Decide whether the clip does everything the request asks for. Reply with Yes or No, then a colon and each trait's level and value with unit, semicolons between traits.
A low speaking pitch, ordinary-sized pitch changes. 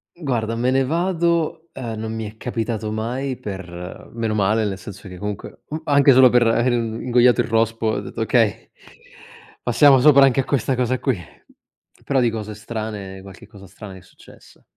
Yes: low, 115 Hz; average, 3.6 semitones